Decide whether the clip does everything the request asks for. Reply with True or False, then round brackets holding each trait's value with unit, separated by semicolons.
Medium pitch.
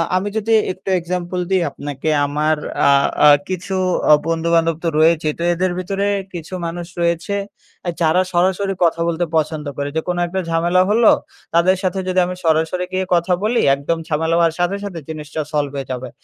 True (170 Hz)